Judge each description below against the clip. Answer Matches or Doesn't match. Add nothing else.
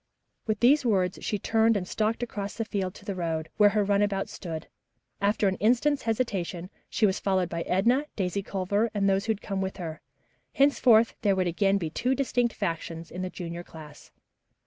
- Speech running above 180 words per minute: Matches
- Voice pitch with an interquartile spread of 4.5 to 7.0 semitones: Doesn't match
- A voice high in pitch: Matches